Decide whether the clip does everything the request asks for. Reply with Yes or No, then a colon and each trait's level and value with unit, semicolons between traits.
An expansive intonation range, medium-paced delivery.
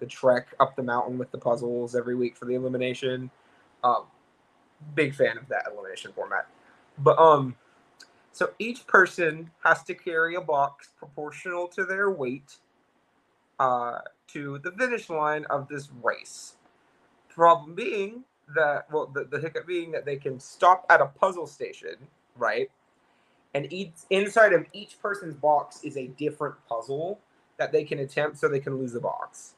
Yes: wide, 6.9 semitones; average, 160 wpm